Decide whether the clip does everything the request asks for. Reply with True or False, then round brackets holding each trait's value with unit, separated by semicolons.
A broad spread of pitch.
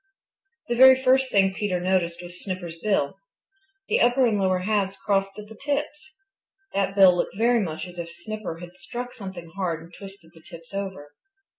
False (3.7 semitones)